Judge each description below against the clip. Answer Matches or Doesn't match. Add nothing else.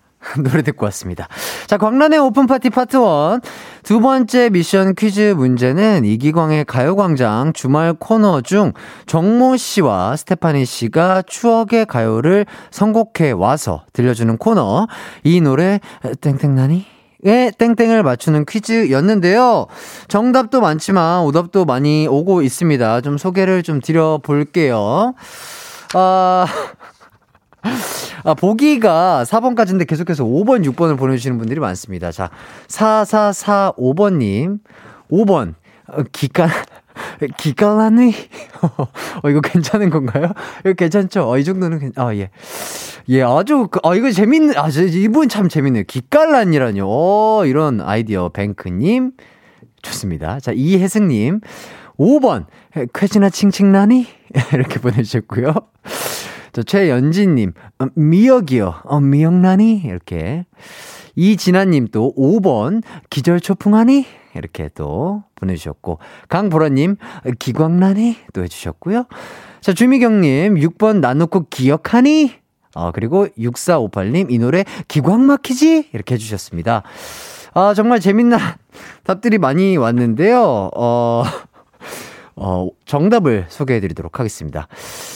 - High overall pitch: Doesn't match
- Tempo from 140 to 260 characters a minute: Matches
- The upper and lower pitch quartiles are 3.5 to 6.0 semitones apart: Doesn't match